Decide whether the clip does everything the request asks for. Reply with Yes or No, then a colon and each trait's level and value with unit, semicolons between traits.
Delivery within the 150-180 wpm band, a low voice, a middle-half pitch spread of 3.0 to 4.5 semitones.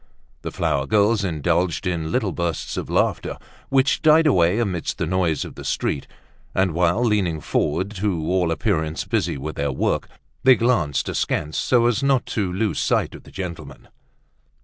No: average, 170 wpm; very low, 90 Hz; average, 5.2 semitones